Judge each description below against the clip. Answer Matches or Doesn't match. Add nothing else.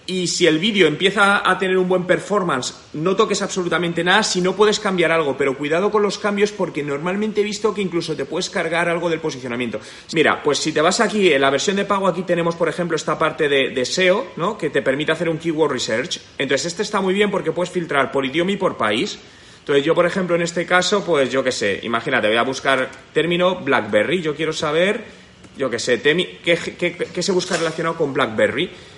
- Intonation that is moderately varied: Matches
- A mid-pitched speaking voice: Matches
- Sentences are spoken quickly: Matches